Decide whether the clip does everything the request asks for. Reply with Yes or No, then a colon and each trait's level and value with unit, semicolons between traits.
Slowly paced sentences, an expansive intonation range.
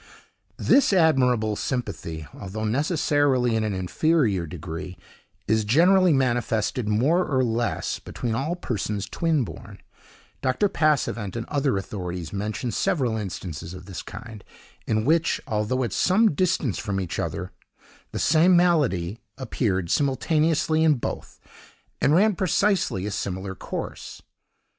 Yes: slow, 130 wpm; wide, 7.5 semitones